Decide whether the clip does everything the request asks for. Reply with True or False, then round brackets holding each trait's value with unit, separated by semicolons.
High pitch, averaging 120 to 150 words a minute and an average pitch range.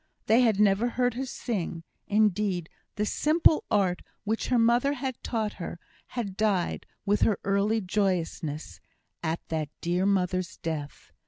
True (205 Hz; 145 wpm; 4.2 semitones)